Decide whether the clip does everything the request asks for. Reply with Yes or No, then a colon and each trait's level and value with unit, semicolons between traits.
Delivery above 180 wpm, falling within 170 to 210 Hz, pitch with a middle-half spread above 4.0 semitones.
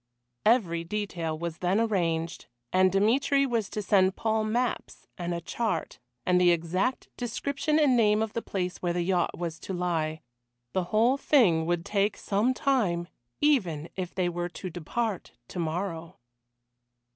No: average, 155 wpm; medium, 185 Hz; average, 4.5 semitones